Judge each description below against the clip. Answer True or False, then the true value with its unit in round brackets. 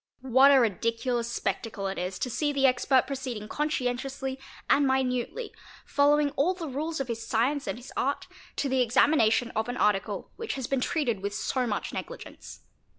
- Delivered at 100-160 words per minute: False (175 wpm)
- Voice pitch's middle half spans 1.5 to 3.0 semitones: False (3.4 semitones)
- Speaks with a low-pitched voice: False (260 Hz)